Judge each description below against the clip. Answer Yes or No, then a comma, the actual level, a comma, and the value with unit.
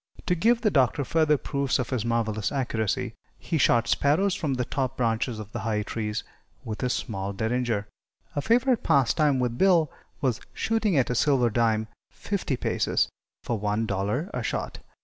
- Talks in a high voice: No, low, 125 Hz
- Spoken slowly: No, average, 170 wpm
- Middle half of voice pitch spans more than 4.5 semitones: Yes, average, 5.3 semitones